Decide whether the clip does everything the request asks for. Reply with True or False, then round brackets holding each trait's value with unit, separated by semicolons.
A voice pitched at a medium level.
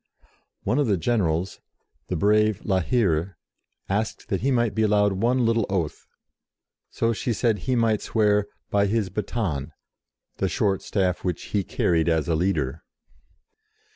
False (100 Hz)